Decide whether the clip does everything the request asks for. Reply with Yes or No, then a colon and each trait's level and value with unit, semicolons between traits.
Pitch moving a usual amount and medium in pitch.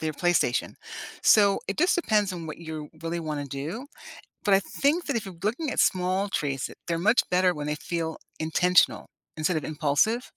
Yes: average, 4.6 semitones; medium, 175 Hz